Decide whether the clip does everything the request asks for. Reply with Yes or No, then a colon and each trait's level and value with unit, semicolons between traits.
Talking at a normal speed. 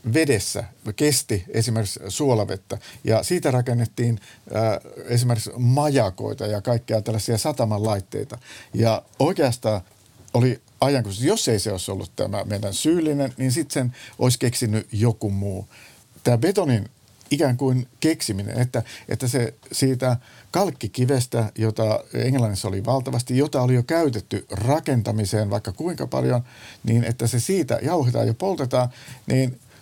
Yes: average, 130 wpm